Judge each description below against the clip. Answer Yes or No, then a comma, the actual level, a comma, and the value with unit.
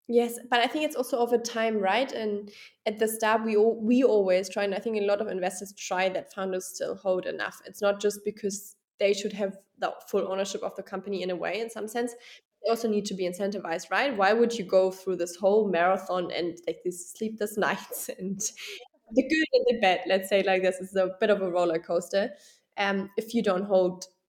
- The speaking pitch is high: Yes, high, 200 Hz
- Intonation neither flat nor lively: Yes, average, 3.1 semitones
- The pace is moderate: No, fast, 230 wpm